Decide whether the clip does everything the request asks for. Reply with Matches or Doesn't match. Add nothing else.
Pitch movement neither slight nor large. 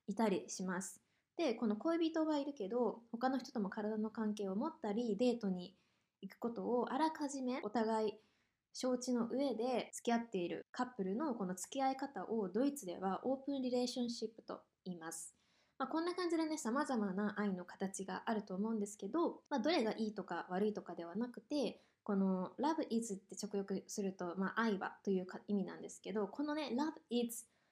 Matches